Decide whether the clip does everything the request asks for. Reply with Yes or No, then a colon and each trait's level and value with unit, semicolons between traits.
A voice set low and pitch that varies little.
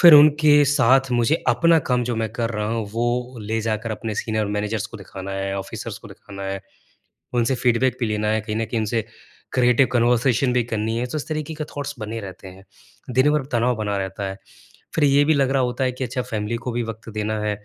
No: low, 115 Hz; average, 3.4 semitones